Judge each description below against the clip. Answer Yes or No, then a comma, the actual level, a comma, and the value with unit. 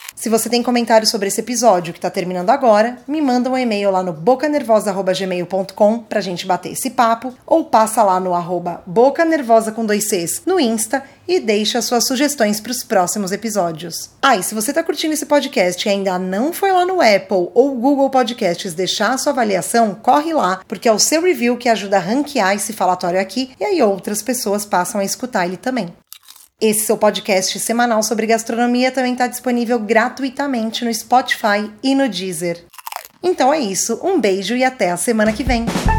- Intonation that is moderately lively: Yes, average, 4.7 semitones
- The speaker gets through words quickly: Yes, fast, 190 wpm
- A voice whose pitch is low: No, high, 225 Hz